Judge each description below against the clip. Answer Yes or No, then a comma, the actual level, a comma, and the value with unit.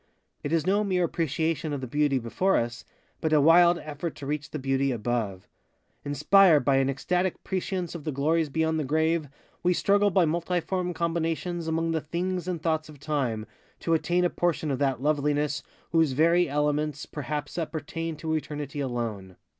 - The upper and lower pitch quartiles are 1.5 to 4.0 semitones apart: Yes, average, 3.1 semitones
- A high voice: No, medium, 155 Hz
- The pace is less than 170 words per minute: No, average, 175 wpm